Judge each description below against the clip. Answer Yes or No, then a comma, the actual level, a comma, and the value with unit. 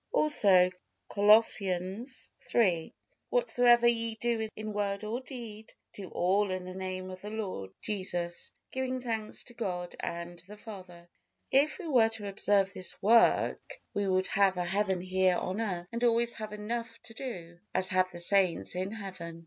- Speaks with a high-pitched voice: Yes, high, 205 Hz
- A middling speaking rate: Yes, average, 165 wpm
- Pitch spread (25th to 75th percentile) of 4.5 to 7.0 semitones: No, average, 3.7 semitones